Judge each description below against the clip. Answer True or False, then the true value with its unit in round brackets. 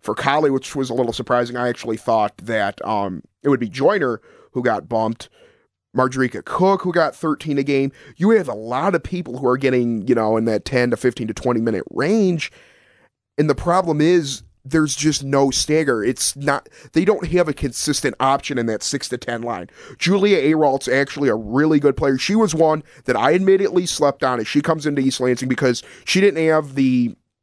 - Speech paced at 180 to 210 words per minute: True (205 wpm)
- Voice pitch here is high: False (135 Hz)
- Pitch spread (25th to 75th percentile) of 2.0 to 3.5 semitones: False (4.3 semitones)